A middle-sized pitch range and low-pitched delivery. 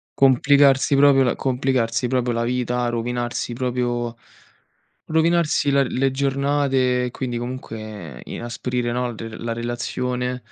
No: narrow, 2.1 semitones; low, 125 Hz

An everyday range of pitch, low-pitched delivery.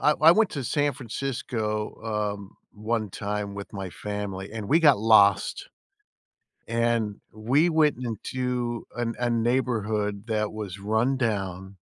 Yes: average, 3.2 semitones; low, 110 Hz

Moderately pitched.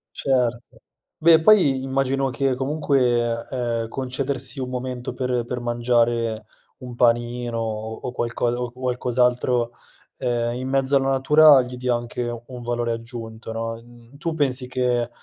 No: low, 125 Hz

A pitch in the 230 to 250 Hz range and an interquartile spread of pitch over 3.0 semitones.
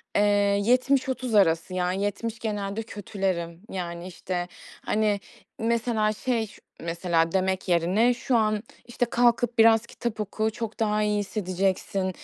No: high, 210 Hz; average, 3.5 semitones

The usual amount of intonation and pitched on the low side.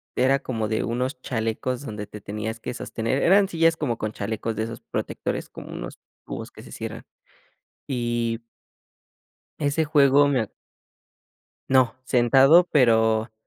Yes: average, 3.7 semitones; low, 120 Hz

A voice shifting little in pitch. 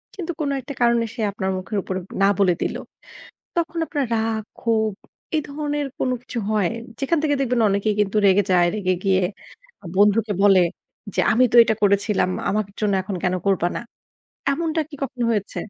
No: average, 5.2 semitones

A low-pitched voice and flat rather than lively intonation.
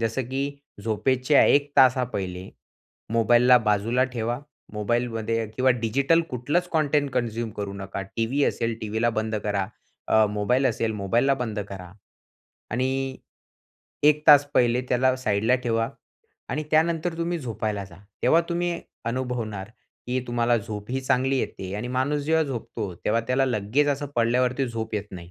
No: low, 120 Hz; average, 3.5 semitones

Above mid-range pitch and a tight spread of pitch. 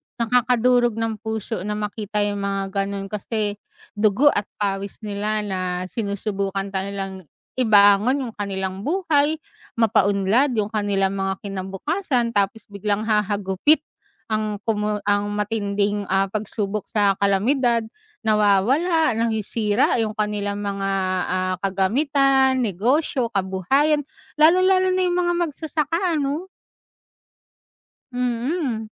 No: high, 210 Hz; average, 3.9 semitones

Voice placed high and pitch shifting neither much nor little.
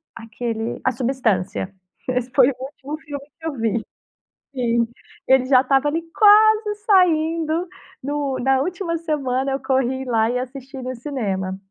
Yes: very high, 265 Hz; average, 3.9 semitones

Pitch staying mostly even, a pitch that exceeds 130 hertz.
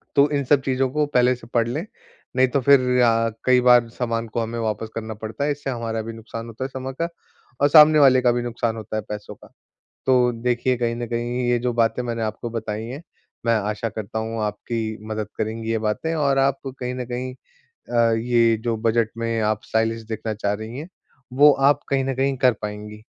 No: narrow, 2.3 semitones; low, 120 Hz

